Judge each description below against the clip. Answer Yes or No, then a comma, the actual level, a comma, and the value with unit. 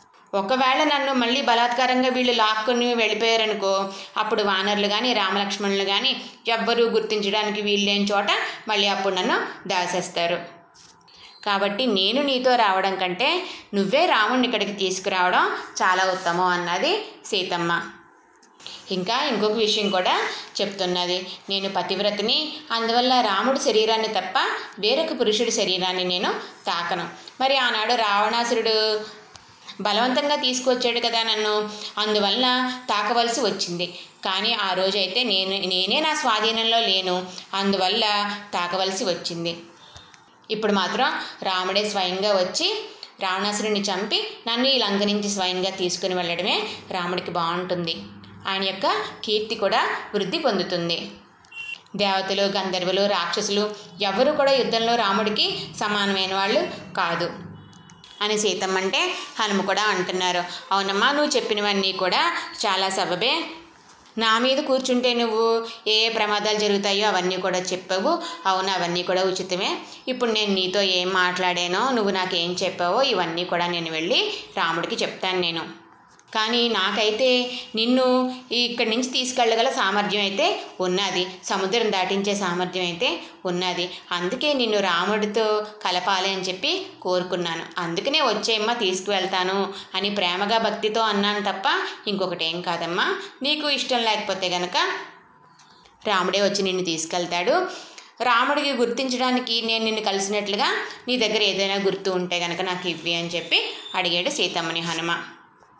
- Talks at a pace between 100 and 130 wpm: Yes, average, 115 wpm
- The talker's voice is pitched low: No, high, 205 Hz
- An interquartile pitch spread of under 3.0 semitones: No, average, 4.1 semitones